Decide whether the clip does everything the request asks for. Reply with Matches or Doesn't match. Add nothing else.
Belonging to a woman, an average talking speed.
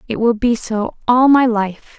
Doesn't match